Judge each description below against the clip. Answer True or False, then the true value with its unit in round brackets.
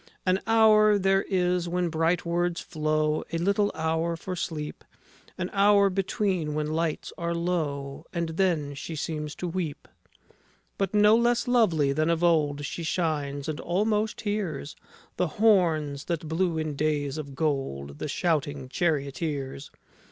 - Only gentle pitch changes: False (3.6 semitones)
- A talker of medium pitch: True (165 Hz)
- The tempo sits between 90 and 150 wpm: True (145 wpm)